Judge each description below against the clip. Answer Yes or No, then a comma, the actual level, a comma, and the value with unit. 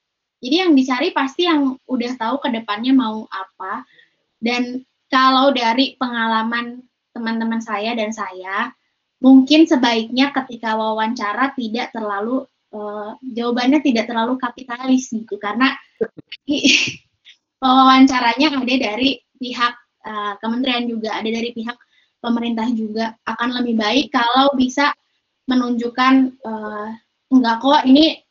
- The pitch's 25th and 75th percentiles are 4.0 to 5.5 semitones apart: No, average, 2.8 semitones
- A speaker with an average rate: Yes, average, 115 wpm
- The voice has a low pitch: No, high, 245 Hz